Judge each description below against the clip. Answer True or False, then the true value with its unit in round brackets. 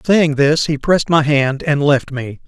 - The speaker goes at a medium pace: False (220 wpm)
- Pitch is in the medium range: True (150 Hz)